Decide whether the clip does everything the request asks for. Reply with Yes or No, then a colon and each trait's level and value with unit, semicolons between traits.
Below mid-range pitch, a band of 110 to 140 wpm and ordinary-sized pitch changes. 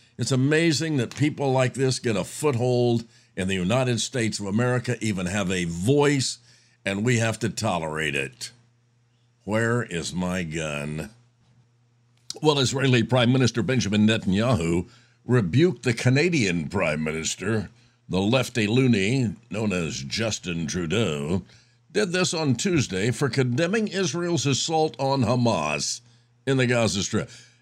Yes: low, 120 Hz; slow, 135 wpm; average, 3.5 semitones